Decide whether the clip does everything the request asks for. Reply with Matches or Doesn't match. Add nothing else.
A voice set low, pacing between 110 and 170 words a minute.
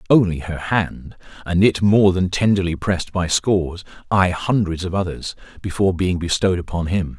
Matches